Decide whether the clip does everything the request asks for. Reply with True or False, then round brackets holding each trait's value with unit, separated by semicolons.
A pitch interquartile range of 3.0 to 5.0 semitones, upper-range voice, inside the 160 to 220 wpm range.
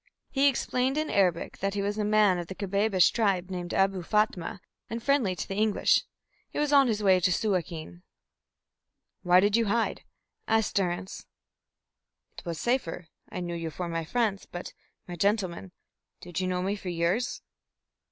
True (3.5 semitones; 195 Hz; 170 wpm)